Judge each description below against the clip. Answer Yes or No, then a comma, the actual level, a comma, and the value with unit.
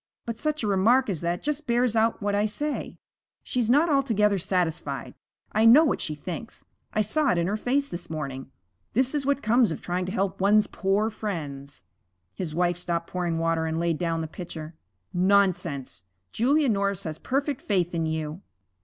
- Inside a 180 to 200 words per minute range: Yes, average, 185 wpm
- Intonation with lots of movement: Yes, wide, 6.0 semitones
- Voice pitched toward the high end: Yes, high, 195 Hz